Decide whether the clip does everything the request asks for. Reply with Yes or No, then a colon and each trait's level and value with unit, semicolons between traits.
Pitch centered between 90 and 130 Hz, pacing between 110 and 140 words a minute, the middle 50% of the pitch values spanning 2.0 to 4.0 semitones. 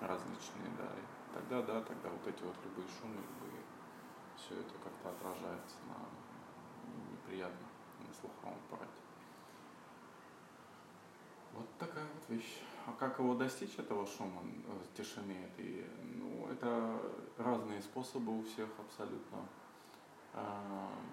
Yes: low, 115 Hz; average, 120 wpm; average, 3.2 semitones